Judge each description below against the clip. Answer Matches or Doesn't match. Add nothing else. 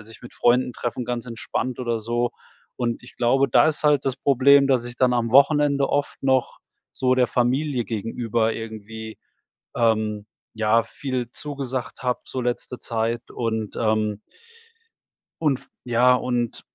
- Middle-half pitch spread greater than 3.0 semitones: Doesn't match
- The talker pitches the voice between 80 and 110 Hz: Doesn't match